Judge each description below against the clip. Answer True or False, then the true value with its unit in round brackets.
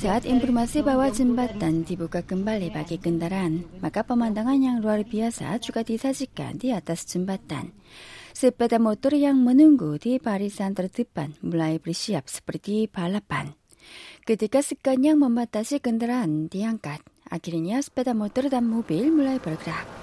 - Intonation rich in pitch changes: True (6.8 semitones)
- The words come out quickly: False (125 wpm)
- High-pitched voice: True (220 Hz)